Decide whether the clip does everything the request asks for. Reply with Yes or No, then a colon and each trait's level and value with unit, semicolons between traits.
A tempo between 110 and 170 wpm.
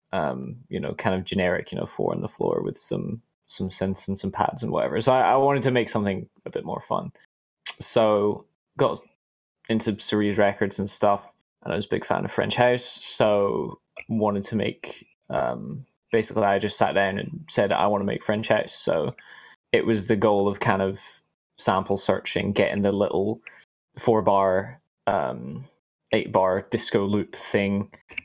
No: average, 180 wpm